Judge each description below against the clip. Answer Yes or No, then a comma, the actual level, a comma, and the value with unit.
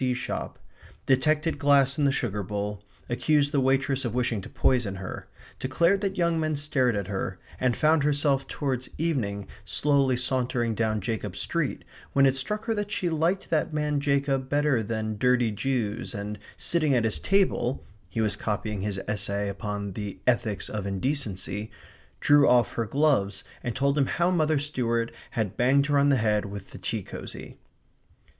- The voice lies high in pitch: No, low, 130 Hz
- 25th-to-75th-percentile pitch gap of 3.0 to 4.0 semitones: No, wide, 5.4 semitones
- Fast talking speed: No, average, 175 wpm